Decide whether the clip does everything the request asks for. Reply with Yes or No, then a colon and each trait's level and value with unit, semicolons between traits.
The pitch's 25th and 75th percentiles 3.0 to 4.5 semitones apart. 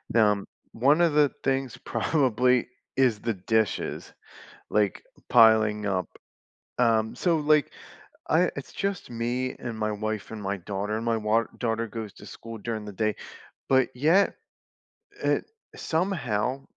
Yes: average, 3.6 semitones